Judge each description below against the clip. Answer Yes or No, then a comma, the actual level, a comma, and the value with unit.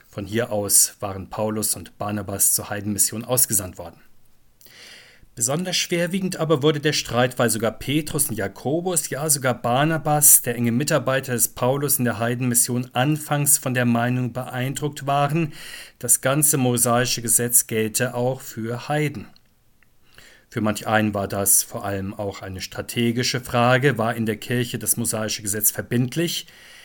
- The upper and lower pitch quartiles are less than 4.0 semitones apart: No, average, 4.4 semitones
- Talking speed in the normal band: Yes, average, 150 wpm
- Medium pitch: No, low, 120 Hz